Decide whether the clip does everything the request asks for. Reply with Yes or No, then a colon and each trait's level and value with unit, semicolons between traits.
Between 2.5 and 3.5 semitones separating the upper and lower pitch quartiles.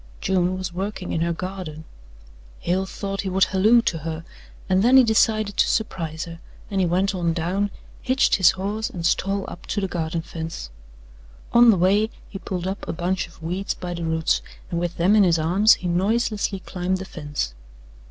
Yes: average, 2.8 semitones